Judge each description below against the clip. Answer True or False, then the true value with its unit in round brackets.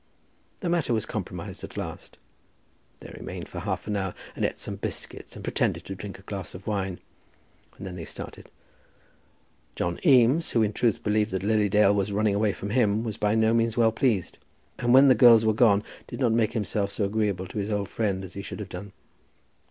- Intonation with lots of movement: False (2.4 semitones)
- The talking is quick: True (210 wpm)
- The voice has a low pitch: True (105 Hz)